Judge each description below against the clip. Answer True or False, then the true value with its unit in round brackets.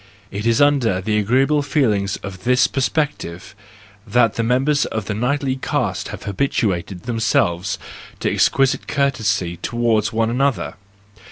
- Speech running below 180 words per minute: True (140 wpm)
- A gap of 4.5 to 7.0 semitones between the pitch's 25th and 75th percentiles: True (4.9 semitones)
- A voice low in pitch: True (115 Hz)